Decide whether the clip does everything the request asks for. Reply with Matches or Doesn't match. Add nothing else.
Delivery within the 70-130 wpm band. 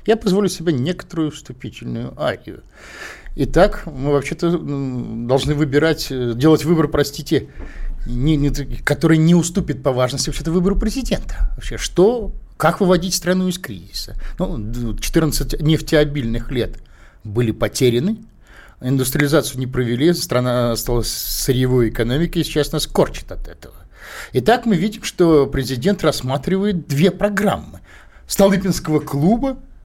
Matches